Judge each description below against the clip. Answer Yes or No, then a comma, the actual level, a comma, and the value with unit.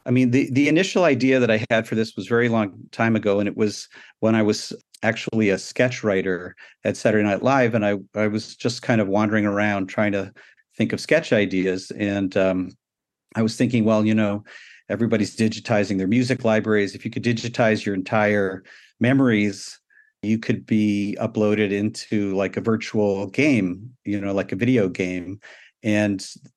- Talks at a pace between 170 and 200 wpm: Yes, average, 185 wpm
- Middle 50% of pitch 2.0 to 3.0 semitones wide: Yes, average, 2.7 semitones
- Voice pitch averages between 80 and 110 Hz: Yes, low, 105 Hz